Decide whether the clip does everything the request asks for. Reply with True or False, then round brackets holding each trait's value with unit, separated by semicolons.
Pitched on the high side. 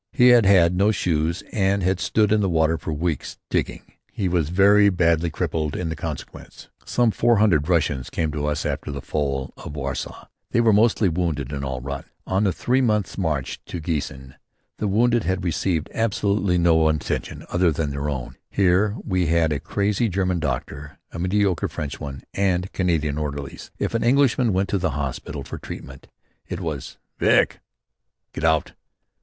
False (85 Hz)